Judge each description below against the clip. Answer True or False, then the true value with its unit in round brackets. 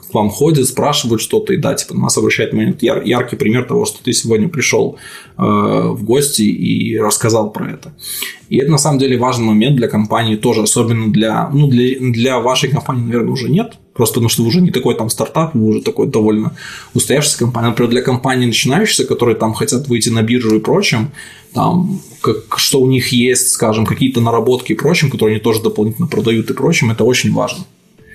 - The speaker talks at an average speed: False (195 wpm)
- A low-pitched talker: True (120 Hz)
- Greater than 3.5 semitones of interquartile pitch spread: False (2.9 semitones)